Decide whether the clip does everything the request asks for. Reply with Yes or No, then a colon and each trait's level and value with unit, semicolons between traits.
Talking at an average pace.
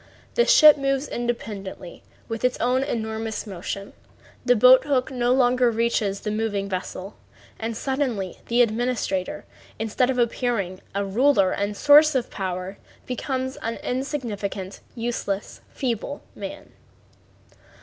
No: slow, 130 wpm